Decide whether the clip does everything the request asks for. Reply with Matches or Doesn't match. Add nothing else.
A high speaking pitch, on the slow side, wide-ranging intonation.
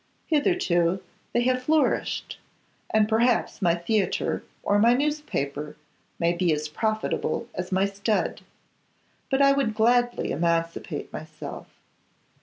Matches